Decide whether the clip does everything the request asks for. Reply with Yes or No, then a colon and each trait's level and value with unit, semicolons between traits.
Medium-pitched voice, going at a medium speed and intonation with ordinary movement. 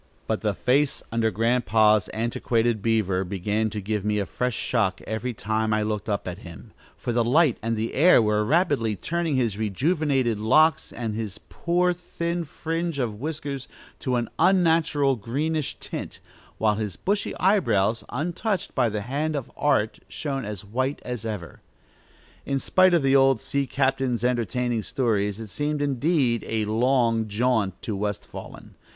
No: low, 120 Hz; average, 160 wpm; average, 5.0 semitones